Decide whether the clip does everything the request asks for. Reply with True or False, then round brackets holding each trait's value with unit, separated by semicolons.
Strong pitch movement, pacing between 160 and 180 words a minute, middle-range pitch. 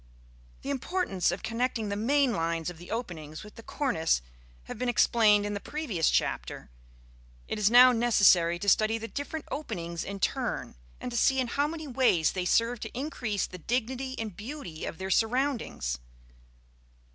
False (6.0 semitones; 170 wpm; 225 Hz)